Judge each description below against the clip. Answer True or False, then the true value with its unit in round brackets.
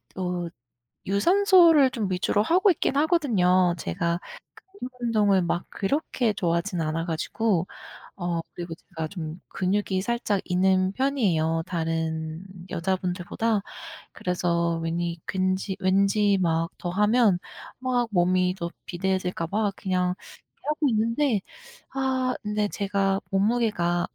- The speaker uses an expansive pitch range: False (4.2 semitones)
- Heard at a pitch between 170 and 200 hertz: True (190 Hz)